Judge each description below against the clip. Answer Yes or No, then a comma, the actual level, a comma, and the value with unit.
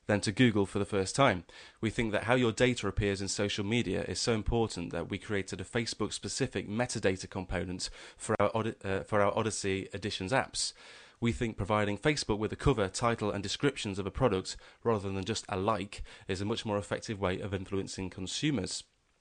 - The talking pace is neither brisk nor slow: Yes, average, 195 wpm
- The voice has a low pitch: Yes, low, 100 Hz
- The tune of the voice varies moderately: Yes, average, 3.0 semitones